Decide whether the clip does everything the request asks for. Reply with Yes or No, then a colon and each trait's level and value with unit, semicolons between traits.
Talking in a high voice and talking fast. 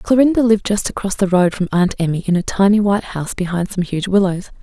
Yes: high, 195 Hz; fast, 235 wpm